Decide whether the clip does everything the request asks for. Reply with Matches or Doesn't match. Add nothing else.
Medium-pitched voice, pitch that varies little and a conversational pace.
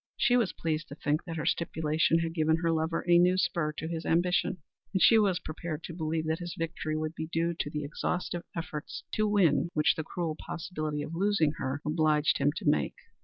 Doesn't match